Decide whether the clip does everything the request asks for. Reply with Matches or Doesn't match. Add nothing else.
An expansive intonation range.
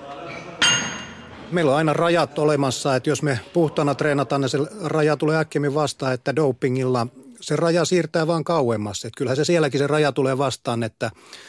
Doesn't match